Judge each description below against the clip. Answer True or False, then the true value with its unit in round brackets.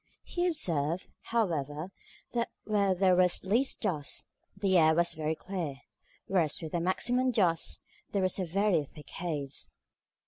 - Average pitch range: True (4.1 semitones)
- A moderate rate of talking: True (150 wpm)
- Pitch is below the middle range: False (180 Hz)